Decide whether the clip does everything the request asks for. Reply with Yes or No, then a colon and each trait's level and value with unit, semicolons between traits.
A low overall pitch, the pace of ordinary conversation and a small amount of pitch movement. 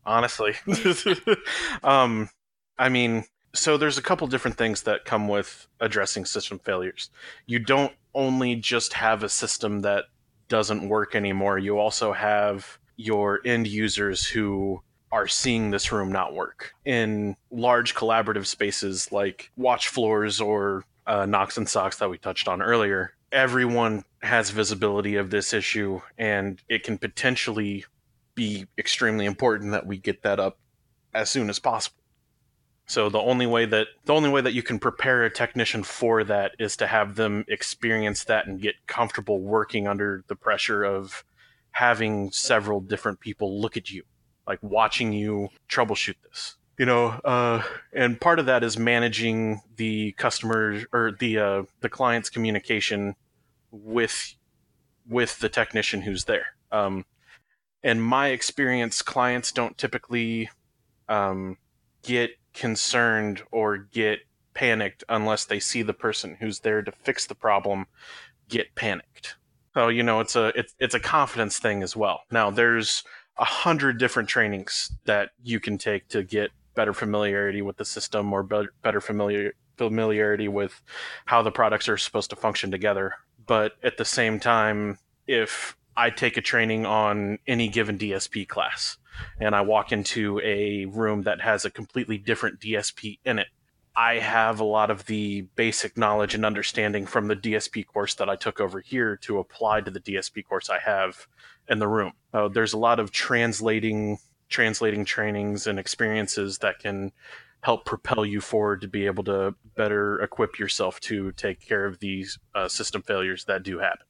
Yes: low, 110 Hz; average, 160 wpm; narrow, 2.2 semitones